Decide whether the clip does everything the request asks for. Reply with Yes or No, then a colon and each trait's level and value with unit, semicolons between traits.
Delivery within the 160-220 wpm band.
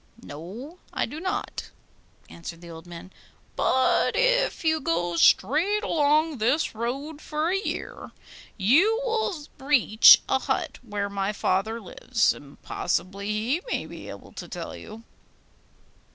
No: slow, 135 wpm